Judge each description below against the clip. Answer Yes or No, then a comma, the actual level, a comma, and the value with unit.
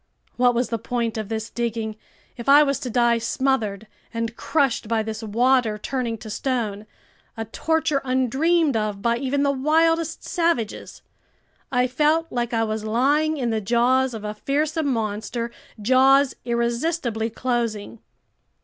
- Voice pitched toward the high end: Yes, high, 240 Hz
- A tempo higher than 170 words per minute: No, average, 150 wpm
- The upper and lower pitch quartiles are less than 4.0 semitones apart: Yes, average, 3.6 semitones